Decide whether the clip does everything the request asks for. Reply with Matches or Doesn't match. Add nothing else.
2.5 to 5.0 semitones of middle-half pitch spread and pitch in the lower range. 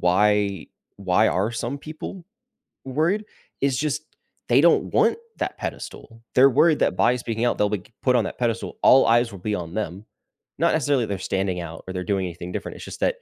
Doesn't match